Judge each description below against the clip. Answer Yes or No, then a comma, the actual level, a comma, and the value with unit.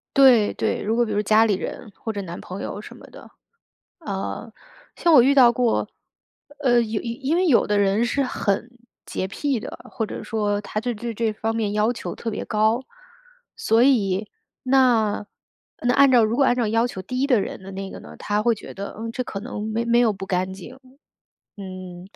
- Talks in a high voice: Yes, high, 225 Hz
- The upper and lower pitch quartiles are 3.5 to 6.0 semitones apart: No, average, 3.1 semitones